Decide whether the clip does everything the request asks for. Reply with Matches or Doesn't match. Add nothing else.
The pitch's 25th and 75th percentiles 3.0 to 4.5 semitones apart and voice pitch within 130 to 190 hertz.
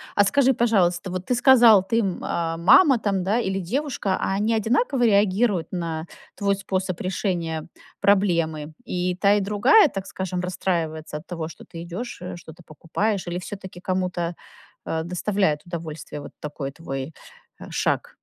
Matches